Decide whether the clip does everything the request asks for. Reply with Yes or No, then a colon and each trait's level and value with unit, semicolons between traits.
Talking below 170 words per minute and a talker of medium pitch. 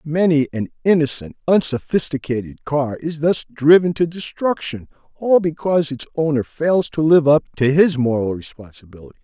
Yes: average, 145 wpm; medium, 145 Hz